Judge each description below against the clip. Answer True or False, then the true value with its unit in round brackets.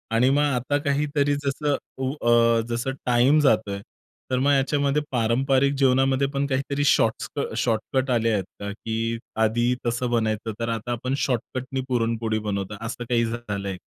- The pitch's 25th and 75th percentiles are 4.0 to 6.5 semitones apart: False (3.1 semitones)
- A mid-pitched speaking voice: False (120 Hz)